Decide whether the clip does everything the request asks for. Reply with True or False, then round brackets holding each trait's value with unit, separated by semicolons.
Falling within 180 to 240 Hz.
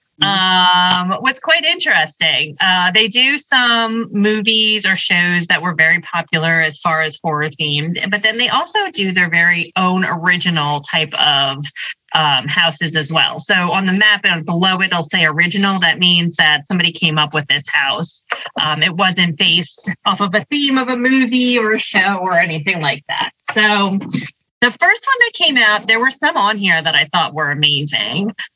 True (185 Hz)